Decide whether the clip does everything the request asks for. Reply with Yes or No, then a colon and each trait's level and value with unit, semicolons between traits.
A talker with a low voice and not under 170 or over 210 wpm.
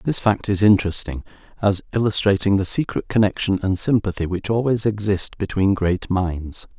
No: low, 100 Hz; average, 150 wpm